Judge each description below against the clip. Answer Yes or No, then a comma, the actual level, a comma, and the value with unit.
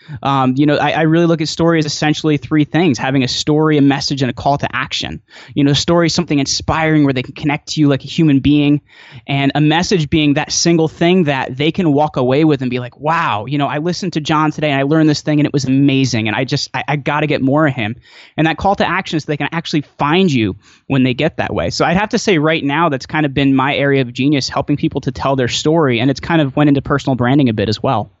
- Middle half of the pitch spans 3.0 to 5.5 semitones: No, narrow, 2.6 semitones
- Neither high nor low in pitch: Yes, medium, 145 Hz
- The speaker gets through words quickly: Yes, fast, 280 wpm